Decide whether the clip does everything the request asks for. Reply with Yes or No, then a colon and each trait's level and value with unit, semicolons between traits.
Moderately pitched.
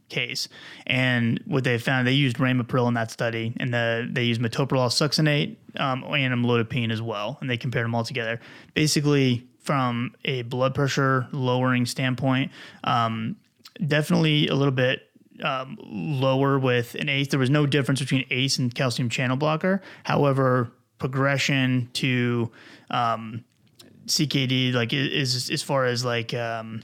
No: low, 130 Hz